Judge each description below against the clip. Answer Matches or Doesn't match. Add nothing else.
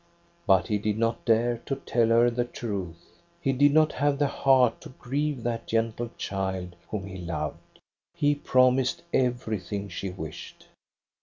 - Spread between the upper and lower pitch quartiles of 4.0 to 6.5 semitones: Matches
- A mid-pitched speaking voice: Doesn't match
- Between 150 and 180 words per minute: Matches